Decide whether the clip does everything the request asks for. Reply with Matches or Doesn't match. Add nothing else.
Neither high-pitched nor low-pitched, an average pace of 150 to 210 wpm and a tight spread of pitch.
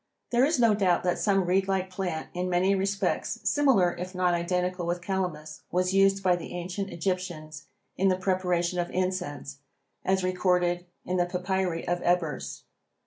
Matches